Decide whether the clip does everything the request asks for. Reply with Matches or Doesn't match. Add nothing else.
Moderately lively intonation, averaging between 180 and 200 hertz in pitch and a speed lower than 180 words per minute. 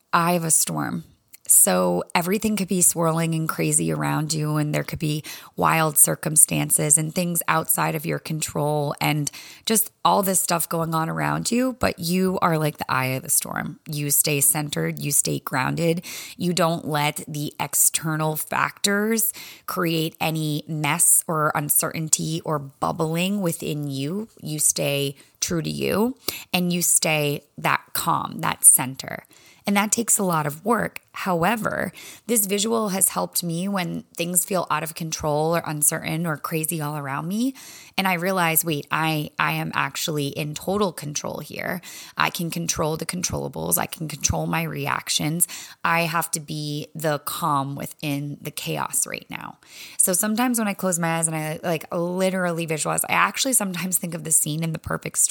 Doesn't match